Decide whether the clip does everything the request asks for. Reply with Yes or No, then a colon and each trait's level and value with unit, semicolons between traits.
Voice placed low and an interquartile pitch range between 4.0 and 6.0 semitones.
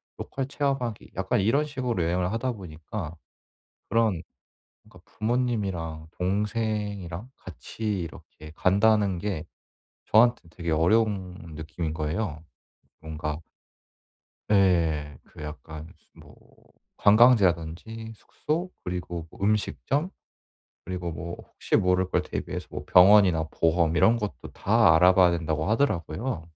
Yes: very low, 90 Hz; average, 5.1 semitones